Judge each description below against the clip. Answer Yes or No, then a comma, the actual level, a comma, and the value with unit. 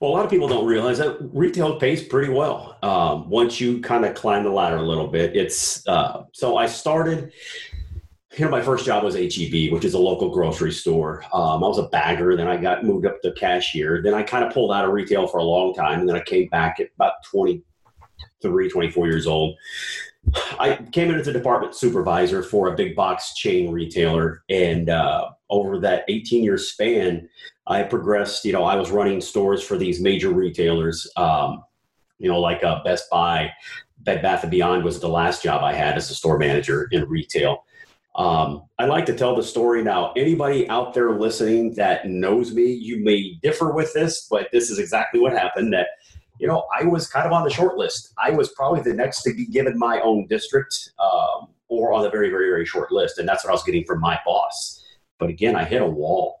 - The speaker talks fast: Yes, fast, 215 wpm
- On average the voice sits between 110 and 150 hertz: Yes, low, 115 Hz